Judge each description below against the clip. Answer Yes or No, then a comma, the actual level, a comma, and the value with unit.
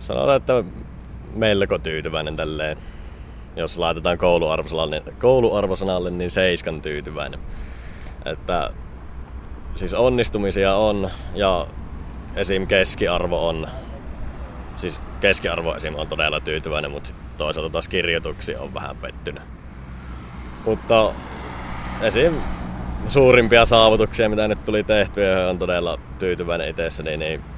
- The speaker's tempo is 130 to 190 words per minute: No, average, 105 wpm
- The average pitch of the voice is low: Yes, very low, 75 Hz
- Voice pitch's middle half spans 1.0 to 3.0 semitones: No, average, 5.0 semitones